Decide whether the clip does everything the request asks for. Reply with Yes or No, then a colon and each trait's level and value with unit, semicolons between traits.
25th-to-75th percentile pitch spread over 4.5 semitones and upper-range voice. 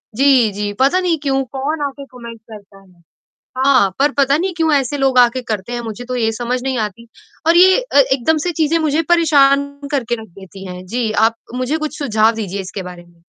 Yes: average, 4.9 semitones; very high, 255 Hz